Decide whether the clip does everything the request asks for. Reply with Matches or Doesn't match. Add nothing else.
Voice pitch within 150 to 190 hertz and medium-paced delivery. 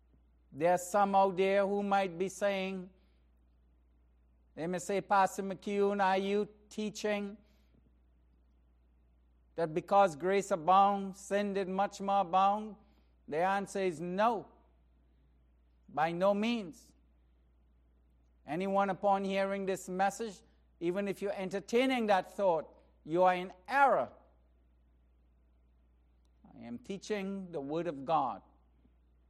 Doesn't match